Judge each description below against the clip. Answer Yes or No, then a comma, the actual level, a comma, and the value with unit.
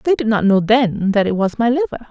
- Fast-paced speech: Yes, fast, 285 wpm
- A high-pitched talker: Yes, high, 225 Hz